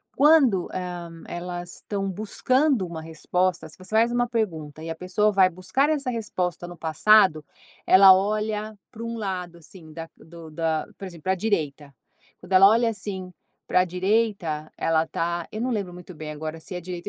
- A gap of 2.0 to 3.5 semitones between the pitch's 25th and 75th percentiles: No, average, 4.3 semitones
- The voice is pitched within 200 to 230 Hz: No, medium, 185 Hz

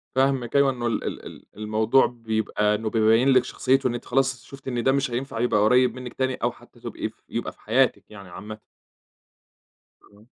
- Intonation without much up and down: No, average, 3.2 semitones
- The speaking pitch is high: No, low, 120 Hz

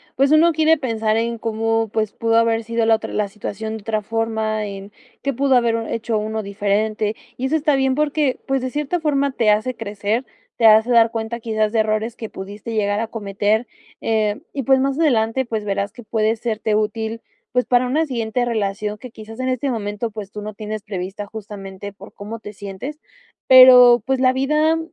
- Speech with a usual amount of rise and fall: Yes, average, 3.1 semitones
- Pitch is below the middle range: No, high, 225 Hz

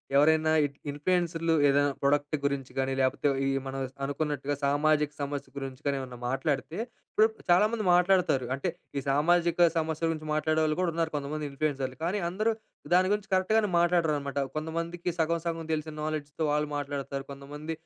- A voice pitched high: No, medium, 155 Hz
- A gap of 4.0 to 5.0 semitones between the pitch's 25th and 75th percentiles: No, average, 3.1 semitones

